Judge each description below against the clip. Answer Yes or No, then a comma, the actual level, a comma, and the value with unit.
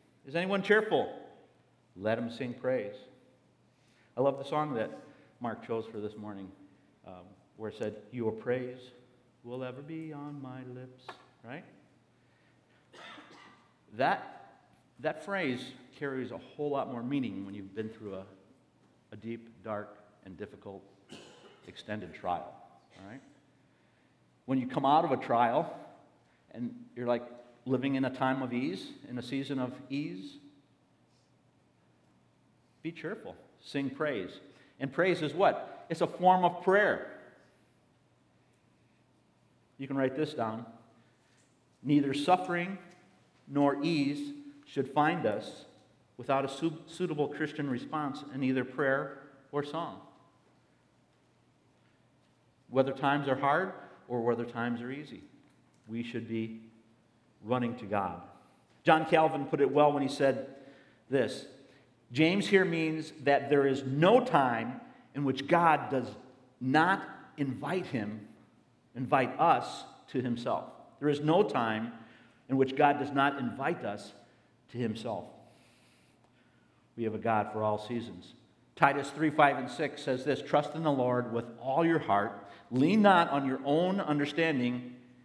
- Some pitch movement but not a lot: Yes, average, 3.9 semitones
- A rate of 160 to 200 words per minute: No, slow, 135 wpm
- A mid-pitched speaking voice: No, low, 130 Hz